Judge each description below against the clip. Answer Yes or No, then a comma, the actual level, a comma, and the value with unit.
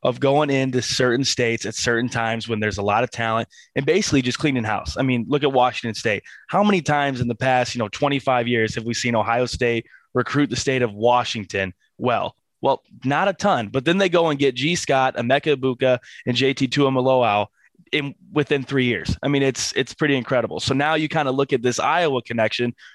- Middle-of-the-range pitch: No, low, 125 Hz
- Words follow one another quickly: Yes, fast, 215 wpm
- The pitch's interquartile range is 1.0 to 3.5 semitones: Yes, average, 3.1 semitones